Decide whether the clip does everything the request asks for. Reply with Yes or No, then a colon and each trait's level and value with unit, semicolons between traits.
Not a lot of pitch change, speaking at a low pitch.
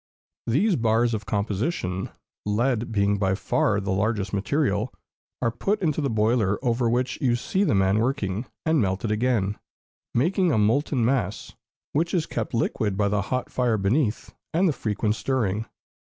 No: average, 4.2 semitones; low, 115 Hz